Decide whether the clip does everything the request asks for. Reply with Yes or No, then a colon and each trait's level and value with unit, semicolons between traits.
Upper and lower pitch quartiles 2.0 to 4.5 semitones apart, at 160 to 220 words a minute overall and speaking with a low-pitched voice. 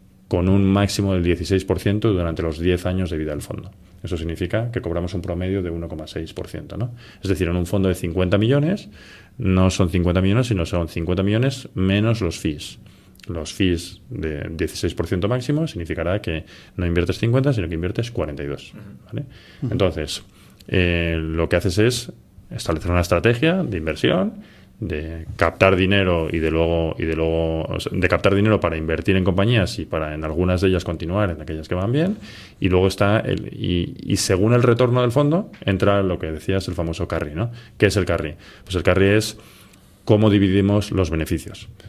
Yes: average, 3.5 semitones; average, 185 wpm; very low, 95 Hz